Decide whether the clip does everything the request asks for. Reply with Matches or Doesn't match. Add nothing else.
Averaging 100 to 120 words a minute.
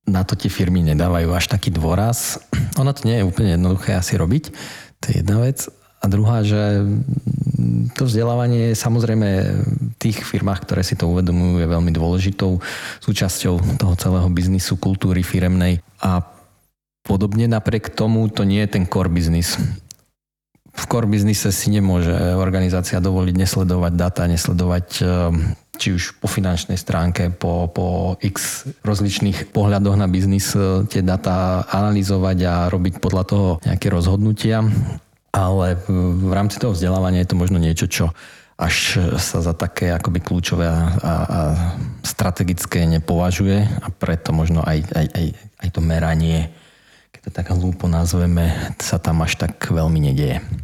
Doesn't match